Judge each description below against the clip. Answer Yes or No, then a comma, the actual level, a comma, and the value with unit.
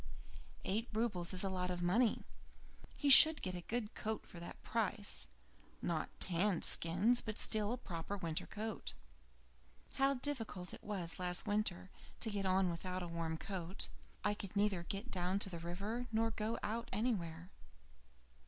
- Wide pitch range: No, average, 3.8 semitones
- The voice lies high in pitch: Yes, high, 195 Hz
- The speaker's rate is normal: Yes, average, 160 wpm